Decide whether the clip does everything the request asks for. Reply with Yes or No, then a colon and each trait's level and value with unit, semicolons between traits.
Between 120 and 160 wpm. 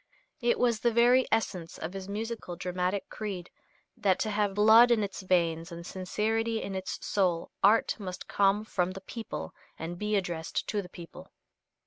No: average, 170 wpm